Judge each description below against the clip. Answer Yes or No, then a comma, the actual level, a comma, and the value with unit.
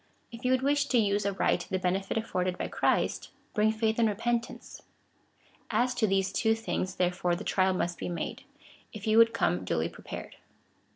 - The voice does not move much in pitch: No, average, 3.8 semitones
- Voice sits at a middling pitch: No, high, 205 Hz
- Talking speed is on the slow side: No, average, 180 wpm